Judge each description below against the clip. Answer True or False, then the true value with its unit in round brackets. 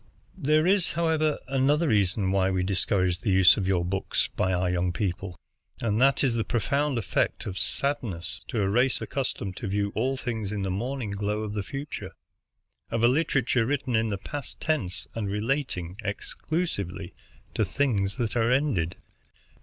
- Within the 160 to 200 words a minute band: True (170 wpm)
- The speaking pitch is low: True (110 Hz)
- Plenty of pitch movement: True (5.9 semitones)